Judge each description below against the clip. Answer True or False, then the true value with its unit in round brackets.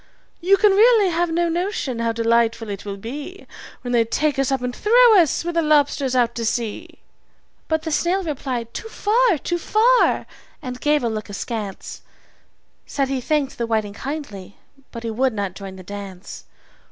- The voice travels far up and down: True (7.0 semitones)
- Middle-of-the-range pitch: False (265 Hz)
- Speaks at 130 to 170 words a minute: False (180 wpm)